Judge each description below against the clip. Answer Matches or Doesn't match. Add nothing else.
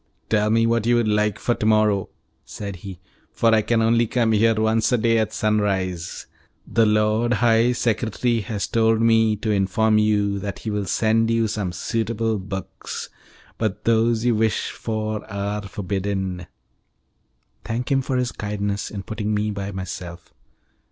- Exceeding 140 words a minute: Matches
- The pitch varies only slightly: Matches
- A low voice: Matches